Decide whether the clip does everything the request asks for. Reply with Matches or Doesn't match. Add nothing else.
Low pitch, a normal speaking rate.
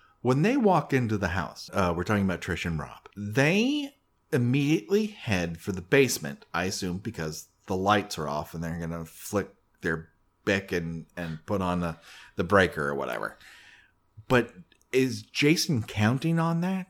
Matches